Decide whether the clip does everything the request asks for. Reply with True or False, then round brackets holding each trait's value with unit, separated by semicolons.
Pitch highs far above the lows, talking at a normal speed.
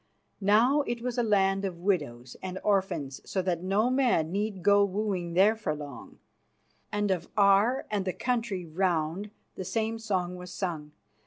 False (3.5 semitones; 165 wpm)